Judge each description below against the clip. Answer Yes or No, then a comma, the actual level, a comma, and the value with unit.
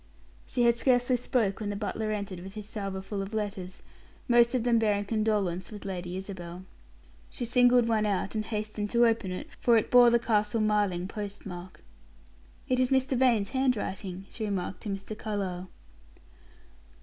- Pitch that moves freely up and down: No, average, 3.3 semitones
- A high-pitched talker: Yes, high, 210 Hz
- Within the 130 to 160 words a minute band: No, average, 175 wpm